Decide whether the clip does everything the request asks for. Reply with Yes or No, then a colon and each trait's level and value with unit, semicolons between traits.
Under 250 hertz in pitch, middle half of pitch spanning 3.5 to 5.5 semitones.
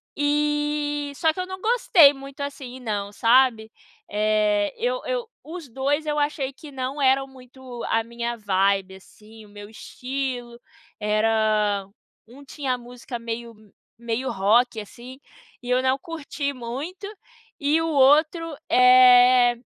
No: very high, 255 Hz; average, 4.3 semitones